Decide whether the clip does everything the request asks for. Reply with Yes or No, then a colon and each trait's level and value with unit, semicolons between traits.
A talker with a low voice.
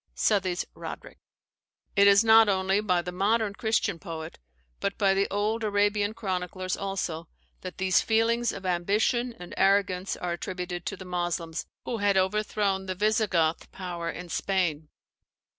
No: high, 195 Hz